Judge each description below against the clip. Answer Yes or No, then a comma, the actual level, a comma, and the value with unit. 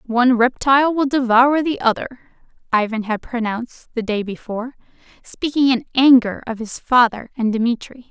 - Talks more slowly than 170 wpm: Yes, average, 150 wpm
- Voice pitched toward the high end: Yes, high, 240 Hz